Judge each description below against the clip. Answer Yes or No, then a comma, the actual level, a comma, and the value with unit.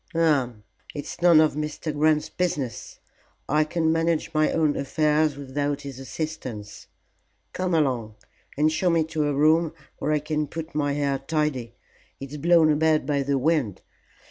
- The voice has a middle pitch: Yes, medium, 150 Hz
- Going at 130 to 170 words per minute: Yes, average, 155 wpm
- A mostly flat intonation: Yes, narrow, 2.3 semitones